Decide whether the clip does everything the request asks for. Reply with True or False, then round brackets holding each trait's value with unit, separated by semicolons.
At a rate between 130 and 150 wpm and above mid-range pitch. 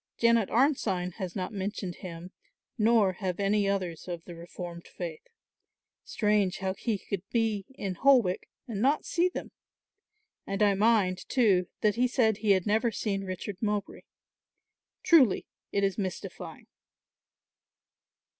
True (135 wpm; 200 Hz)